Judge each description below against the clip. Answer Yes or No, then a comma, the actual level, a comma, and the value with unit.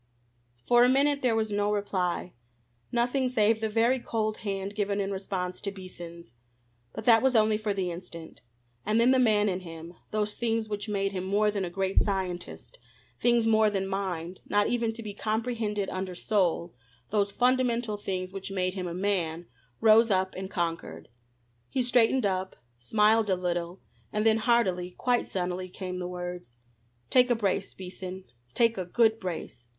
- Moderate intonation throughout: Yes, average, 3.5 semitones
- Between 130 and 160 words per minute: No, average, 175 wpm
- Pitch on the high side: Yes, high, 200 Hz